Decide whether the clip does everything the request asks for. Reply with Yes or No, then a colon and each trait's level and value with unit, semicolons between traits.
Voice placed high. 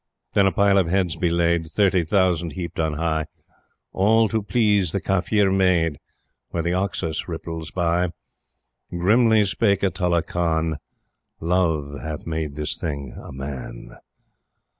No: very low, 85 Hz